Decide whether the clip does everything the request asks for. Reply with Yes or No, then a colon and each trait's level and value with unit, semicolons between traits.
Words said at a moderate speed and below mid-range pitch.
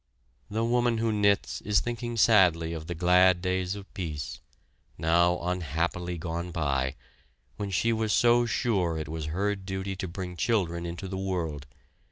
Yes: average, 160 wpm; very low, 90 Hz